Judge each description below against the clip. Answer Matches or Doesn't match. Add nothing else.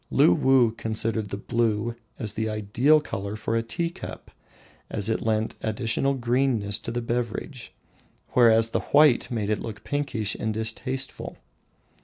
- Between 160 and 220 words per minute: Doesn't match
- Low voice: Matches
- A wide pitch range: Doesn't match